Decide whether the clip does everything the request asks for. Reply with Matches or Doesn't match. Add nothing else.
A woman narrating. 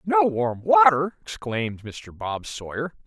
Doesn't match